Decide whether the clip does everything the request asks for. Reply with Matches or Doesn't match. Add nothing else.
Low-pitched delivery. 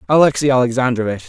Matches